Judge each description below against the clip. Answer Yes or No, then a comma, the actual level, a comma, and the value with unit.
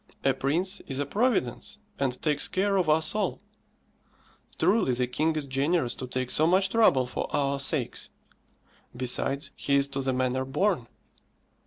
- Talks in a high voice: No, medium, 140 Hz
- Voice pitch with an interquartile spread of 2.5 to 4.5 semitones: No, average, 5.1 semitones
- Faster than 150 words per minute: Yes, average, 160 wpm